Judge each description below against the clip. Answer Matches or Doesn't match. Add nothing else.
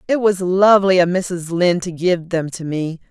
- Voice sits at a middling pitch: Matches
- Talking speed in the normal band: Doesn't match